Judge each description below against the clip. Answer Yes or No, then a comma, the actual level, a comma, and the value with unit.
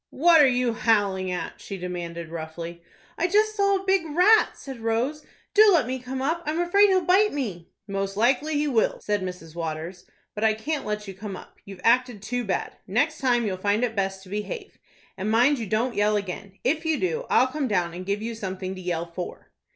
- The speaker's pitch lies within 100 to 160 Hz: No, high, 225 Hz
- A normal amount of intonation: No, wide, 7.8 semitones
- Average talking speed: No, fast, 215 wpm